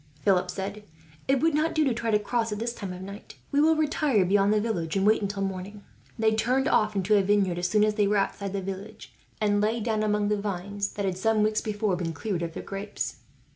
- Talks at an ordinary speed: No, fast, 245 wpm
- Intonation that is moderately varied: No, narrow, 2.1 semitones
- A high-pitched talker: Yes, high, 210 Hz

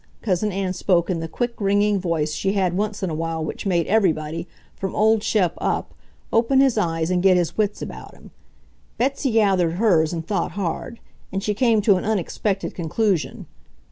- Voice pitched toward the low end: No, high, 195 Hz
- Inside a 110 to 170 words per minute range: No, average, 185 wpm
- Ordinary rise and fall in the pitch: Yes, average, 3.9 semitones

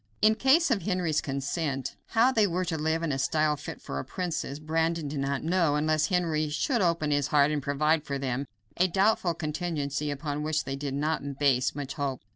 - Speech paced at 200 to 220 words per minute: Yes, fast, 205 wpm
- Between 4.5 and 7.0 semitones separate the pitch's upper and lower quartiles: No, average, 3.3 semitones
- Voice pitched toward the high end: No, medium, 155 Hz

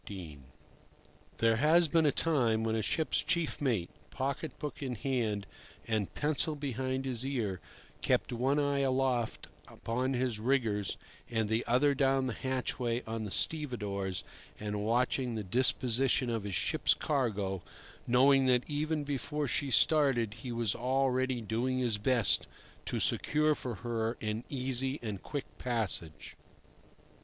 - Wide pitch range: No, average, 3.5 semitones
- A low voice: Yes, low, 125 Hz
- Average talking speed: Yes, average, 145 wpm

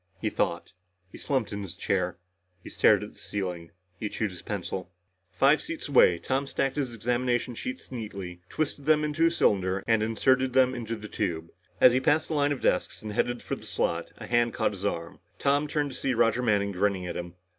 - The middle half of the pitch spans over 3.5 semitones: Yes, wide, 5.6 semitones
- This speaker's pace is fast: Yes, fast, 210 wpm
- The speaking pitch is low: Yes, low, 115 Hz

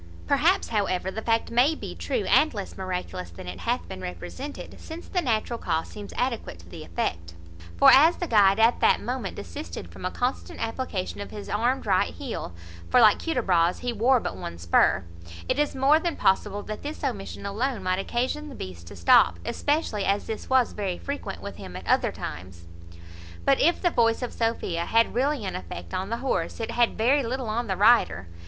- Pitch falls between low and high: No, high, 220 Hz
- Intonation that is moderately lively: No, wide, 6.5 semitones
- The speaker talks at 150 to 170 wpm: No, average, 200 wpm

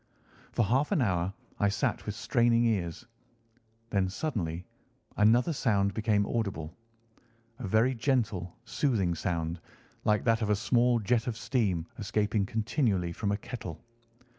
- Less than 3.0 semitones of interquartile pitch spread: No, average, 3.7 semitones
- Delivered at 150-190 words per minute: No, slow, 135 wpm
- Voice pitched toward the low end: Yes, low, 110 Hz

